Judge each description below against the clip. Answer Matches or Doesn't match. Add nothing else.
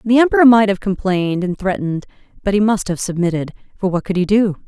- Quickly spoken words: Matches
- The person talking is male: Doesn't match